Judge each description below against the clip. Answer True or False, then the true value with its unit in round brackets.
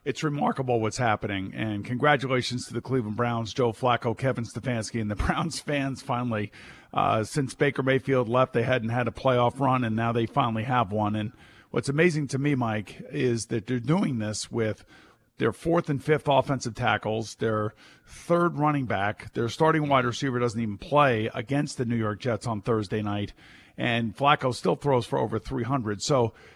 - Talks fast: False (185 wpm)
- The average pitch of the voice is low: True (120 Hz)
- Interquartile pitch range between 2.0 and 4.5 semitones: True (3.5 semitones)